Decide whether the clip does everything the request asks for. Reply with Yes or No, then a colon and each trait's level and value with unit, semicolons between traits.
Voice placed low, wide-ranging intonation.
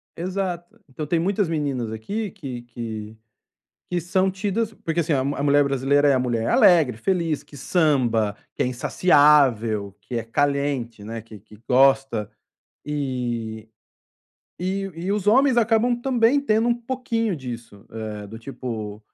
No: medium, 145 Hz; wide, 8.1 semitones